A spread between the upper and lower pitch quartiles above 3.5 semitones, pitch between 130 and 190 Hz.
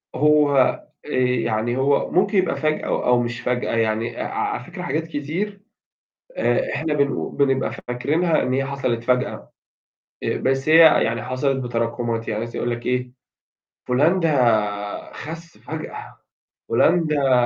Yes: average, 4.1 semitones; low, 135 Hz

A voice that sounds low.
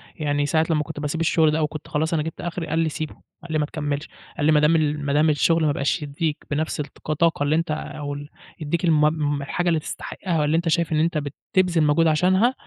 No: medium, 155 Hz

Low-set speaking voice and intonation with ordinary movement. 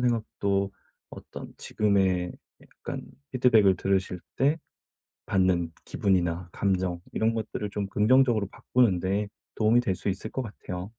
Yes: low, 100 Hz; average, 3.1 semitones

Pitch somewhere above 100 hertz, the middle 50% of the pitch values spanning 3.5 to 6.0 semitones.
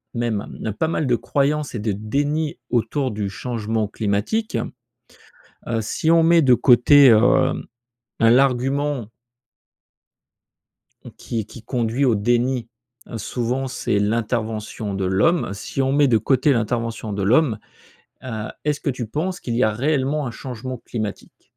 Yes: low, 120 Hz; average, 4.2 semitones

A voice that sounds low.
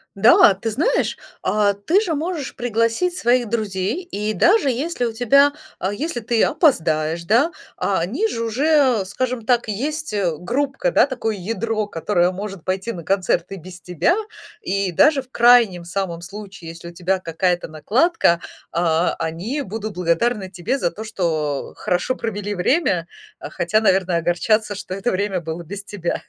No: high, 205 Hz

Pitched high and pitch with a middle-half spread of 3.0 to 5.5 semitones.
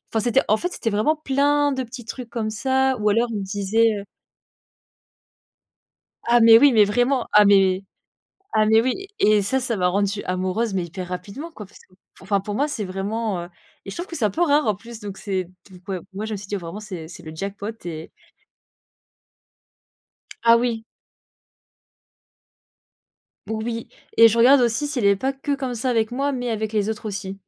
Yes: high, 220 Hz; average, 3.7 semitones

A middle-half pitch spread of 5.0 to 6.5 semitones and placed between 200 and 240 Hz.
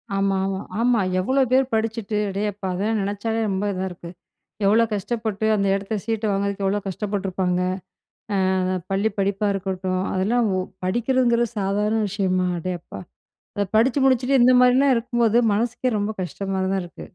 No: average, 3.2 semitones; high, 205 Hz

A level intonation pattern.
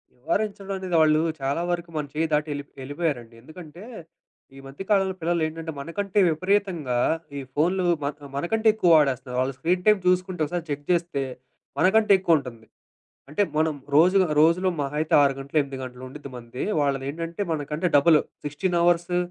No: average, 4.2 semitones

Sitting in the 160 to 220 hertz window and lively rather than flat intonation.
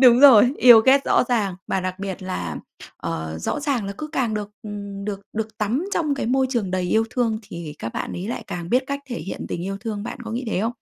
No: high, 215 Hz; average, 4.5 semitones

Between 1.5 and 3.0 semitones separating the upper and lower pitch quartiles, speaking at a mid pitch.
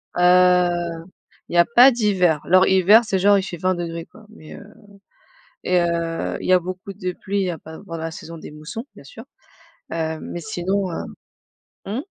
Yes: narrow, 2.6 semitones; medium, 180 Hz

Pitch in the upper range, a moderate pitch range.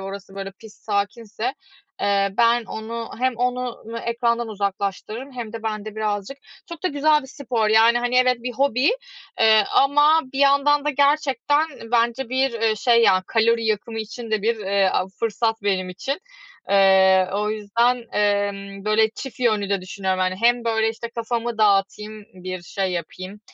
Yes: high, 225 Hz; average, 3.3 semitones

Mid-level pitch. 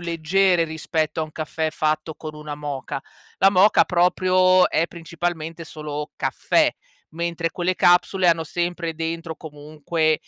Yes: medium, 165 Hz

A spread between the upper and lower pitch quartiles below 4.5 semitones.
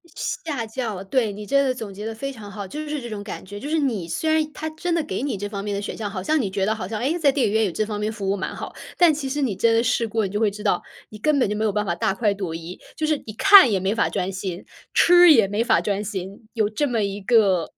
No: average, 5.1 semitones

